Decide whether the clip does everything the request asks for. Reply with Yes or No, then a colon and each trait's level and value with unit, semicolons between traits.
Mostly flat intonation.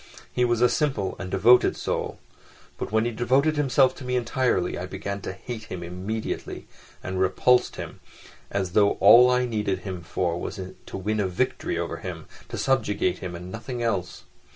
No: average, 4.9 semitones